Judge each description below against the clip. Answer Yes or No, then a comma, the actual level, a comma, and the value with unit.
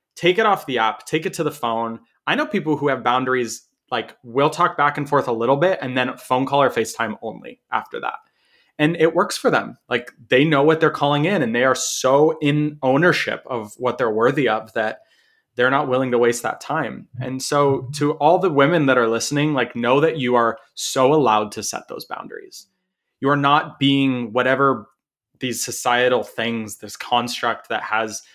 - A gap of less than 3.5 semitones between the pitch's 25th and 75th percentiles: No, average, 4.3 semitones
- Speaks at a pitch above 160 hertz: No, low, 135 Hz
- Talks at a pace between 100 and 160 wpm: No, fast, 205 wpm